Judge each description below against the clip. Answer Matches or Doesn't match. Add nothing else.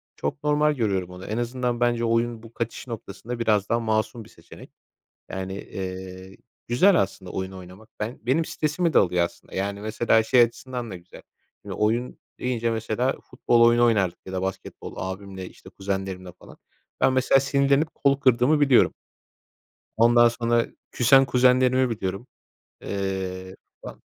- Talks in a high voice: Doesn't match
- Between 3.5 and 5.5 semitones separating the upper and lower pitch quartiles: Matches